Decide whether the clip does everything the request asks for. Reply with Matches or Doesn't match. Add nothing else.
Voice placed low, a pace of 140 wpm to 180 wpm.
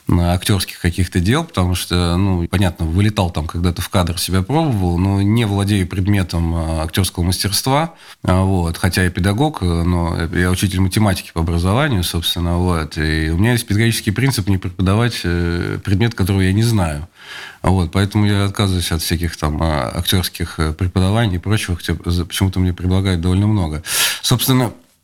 Matches